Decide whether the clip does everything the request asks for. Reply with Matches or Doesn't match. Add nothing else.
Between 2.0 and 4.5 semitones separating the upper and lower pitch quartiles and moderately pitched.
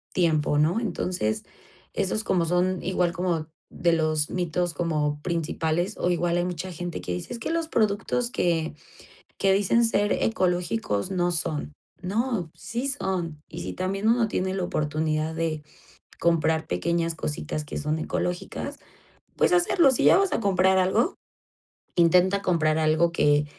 Matches